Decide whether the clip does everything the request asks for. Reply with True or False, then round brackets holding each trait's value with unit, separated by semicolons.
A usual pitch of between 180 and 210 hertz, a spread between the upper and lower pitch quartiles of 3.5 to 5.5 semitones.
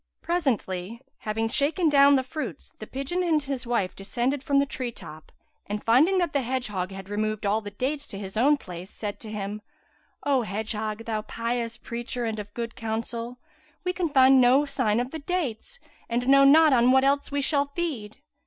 False (245 Hz; 4.7 semitones)